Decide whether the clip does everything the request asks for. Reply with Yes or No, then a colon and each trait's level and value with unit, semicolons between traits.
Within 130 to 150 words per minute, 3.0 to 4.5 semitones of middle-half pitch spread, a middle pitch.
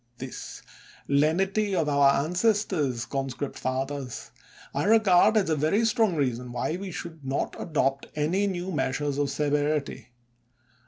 No: average, 145 wpm; wide, 5.4 semitones; medium, 150 Hz